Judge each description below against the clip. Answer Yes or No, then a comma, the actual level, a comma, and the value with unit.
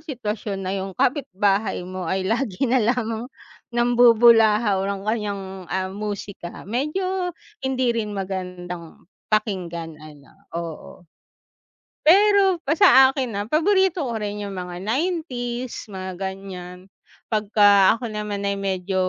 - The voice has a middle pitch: No, high, 210 Hz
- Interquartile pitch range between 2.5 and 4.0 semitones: No, average, 4.5 semitones